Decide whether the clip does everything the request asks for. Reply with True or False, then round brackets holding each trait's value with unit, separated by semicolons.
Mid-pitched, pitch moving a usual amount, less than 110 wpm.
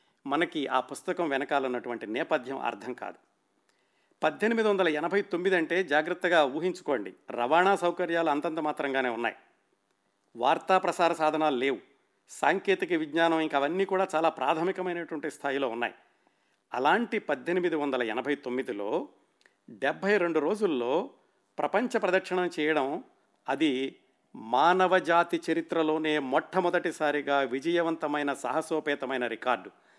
True (160 Hz; 4.1 semitones; 100 wpm)